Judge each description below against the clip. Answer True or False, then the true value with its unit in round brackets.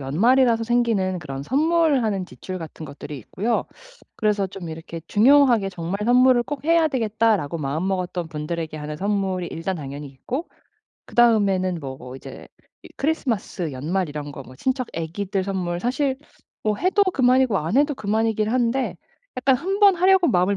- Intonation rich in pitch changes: True (7.3 semitones)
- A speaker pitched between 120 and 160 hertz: False (200 Hz)